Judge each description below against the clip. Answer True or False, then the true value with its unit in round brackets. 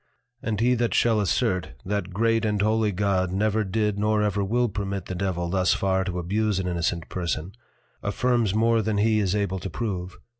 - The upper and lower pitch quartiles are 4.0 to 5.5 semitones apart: False (2.8 semitones)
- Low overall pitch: True (100 Hz)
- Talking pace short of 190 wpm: False (195 wpm)